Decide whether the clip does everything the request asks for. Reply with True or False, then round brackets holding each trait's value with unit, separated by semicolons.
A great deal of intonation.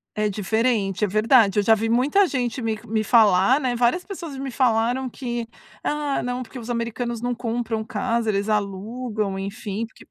False (2.8 semitones)